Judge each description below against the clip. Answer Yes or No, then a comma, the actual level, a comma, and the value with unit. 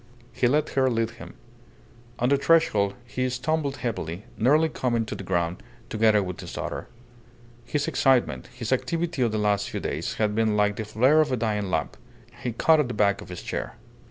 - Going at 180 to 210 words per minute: Yes, average, 195 wpm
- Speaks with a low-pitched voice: Yes, low, 115 Hz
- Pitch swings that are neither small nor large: Yes, average, 4.4 semitones